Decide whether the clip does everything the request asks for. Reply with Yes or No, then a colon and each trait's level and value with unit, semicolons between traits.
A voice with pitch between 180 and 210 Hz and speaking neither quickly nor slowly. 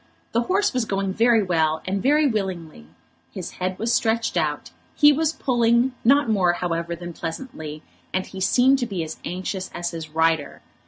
Yes: high, 190 Hz; average, 175 wpm